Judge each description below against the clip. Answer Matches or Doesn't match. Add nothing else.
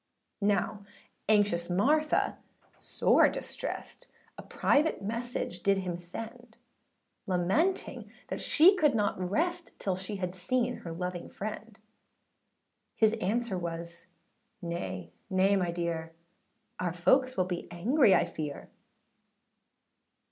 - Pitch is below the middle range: Doesn't match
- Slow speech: Matches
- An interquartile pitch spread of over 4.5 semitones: Matches